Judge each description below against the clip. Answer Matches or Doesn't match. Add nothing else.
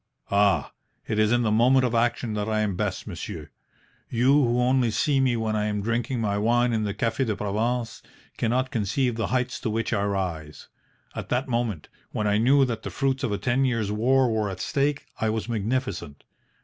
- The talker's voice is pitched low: Matches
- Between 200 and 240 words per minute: Matches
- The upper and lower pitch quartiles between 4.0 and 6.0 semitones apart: Doesn't match